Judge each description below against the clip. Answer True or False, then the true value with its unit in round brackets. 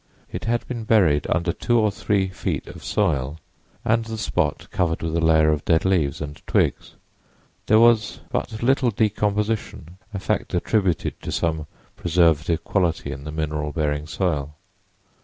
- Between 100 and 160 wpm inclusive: True (155 wpm)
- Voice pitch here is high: False (85 Hz)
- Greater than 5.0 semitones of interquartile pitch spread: True (5.5 semitones)